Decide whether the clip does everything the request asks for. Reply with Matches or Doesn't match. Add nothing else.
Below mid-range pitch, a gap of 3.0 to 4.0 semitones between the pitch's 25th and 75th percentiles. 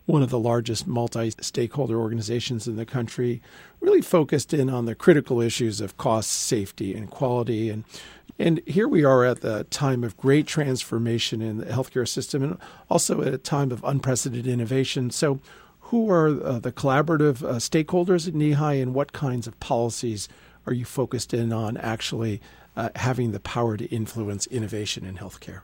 Matches